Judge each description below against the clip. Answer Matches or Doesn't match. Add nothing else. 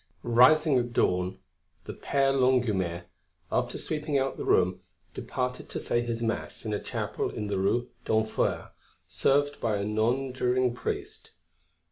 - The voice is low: Matches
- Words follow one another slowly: Doesn't match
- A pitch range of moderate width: Matches